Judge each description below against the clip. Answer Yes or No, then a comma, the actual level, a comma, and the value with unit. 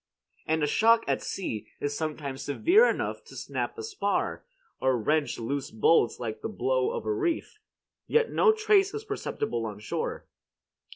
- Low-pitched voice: No, medium, 185 Hz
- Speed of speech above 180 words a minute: No, average, 165 wpm